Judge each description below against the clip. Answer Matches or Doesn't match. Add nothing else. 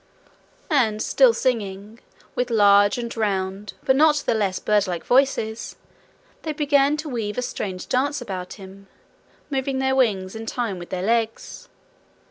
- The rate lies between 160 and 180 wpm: Doesn't match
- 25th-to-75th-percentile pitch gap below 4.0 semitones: Doesn't match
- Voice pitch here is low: Doesn't match